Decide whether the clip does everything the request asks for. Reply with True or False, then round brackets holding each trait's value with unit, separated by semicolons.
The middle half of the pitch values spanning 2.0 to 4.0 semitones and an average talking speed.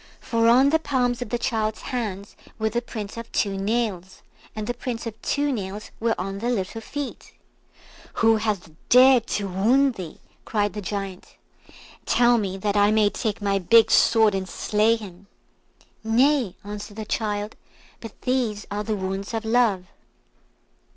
True (2.9 semitones; 165 wpm)